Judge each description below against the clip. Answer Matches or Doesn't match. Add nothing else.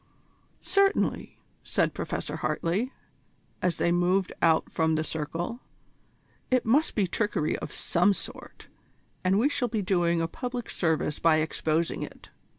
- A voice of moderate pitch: Matches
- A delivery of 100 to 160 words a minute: Matches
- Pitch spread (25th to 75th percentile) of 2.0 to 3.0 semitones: Doesn't match